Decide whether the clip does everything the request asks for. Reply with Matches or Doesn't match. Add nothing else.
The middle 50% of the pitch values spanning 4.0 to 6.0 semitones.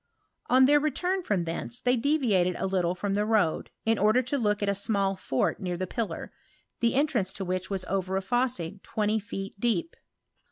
Matches